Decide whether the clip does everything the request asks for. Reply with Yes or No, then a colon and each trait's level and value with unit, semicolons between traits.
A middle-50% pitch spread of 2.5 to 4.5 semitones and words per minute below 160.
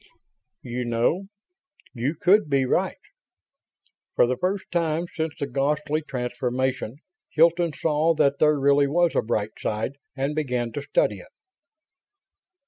Yes: average, 4.1 semitones; slow, 135 wpm